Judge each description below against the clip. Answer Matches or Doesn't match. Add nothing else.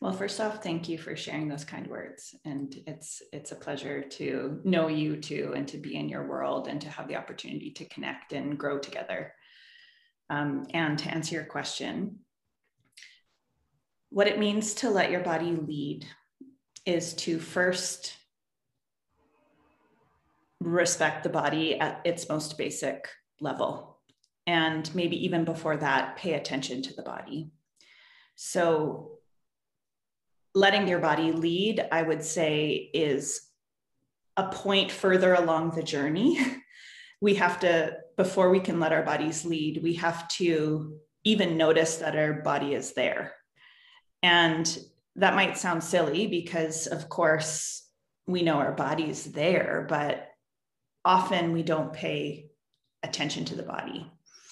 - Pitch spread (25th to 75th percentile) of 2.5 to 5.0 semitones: Matches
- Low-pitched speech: Doesn't match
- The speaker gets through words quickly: Doesn't match